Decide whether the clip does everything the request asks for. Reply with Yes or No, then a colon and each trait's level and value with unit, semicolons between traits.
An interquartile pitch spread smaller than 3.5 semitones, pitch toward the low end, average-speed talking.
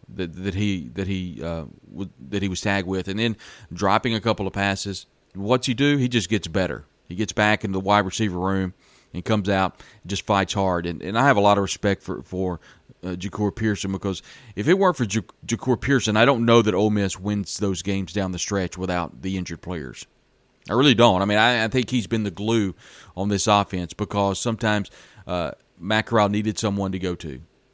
No: narrow, 2.6 semitones; low, 100 Hz; fast, 220 wpm